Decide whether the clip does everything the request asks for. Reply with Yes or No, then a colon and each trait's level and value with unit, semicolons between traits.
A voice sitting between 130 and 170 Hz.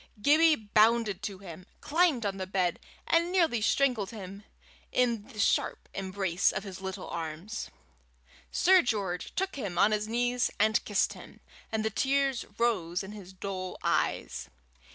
No: high, 210 Hz